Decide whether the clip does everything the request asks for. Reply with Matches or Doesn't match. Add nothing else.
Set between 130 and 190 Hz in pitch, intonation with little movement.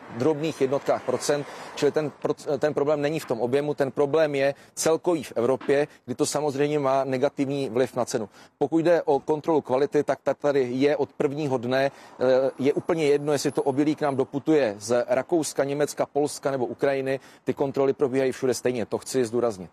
Matches